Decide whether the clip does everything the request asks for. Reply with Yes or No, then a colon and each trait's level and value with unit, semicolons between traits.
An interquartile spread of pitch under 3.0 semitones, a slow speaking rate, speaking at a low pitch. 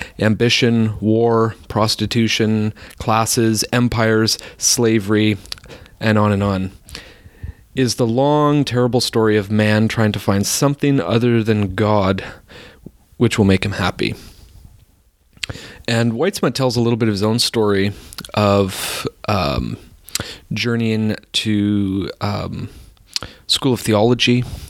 Yes: narrow, 2.6 semitones; slow, 115 wpm; low, 110 Hz